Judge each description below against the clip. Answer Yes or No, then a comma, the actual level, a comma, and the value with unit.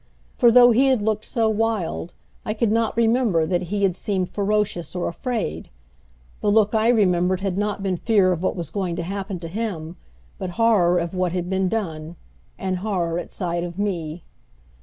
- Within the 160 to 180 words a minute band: No, average, 190 wpm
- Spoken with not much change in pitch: No, average, 3.8 semitones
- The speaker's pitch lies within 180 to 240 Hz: Yes, high, 190 Hz